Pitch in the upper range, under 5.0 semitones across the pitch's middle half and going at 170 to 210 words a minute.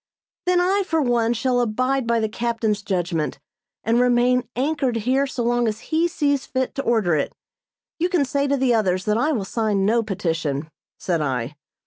Yes: high, 235 Hz; average, 4.5 semitones; average, 185 wpm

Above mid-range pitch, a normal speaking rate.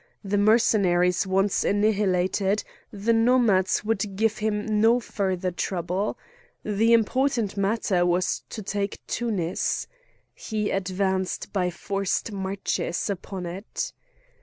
No: high, 200 Hz; slow, 110 wpm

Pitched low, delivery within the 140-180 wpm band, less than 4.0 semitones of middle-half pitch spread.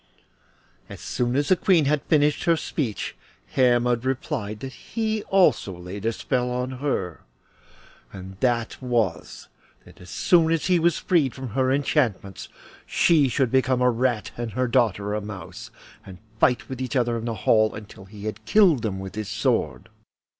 No: low, 125 Hz; average, 170 wpm; average, 4.6 semitones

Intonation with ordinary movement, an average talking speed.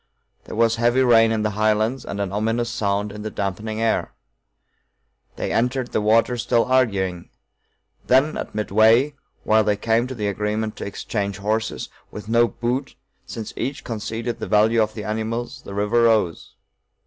No: narrow, 2.0 semitones; average, 165 wpm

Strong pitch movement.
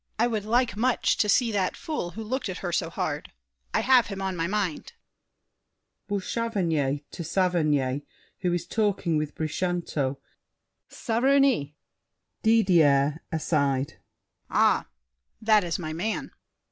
Yes: wide, 5.8 semitones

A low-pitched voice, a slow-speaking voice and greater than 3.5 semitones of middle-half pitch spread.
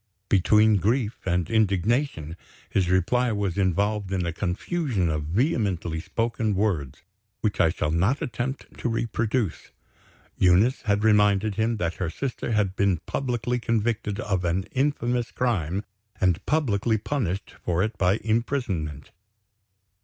Yes: low, 105 Hz; slow, 130 wpm; average, 4.5 semitones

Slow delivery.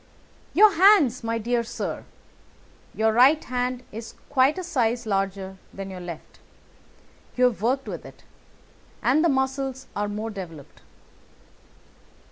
Yes: slow, 130 wpm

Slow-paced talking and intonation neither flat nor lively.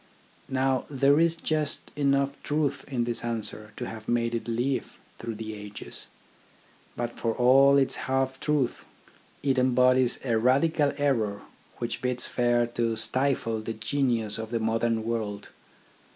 No: average, 145 wpm; average, 3.2 semitones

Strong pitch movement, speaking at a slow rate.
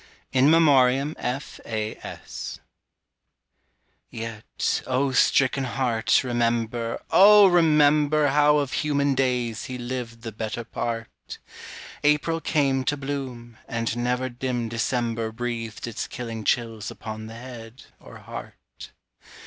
No: average, 3.4 semitones; slow, 110 wpm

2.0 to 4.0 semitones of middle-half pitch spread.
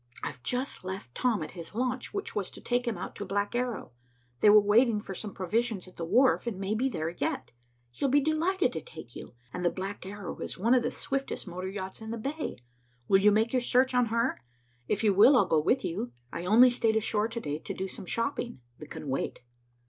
No: average, 4.8 semitones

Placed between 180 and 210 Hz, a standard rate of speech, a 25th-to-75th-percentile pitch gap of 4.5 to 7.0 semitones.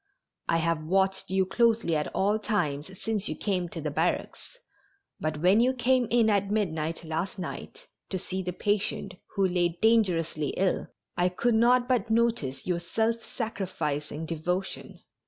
Yes: high, 190 Hz; average, 155 wpm; average, 5.0 semitones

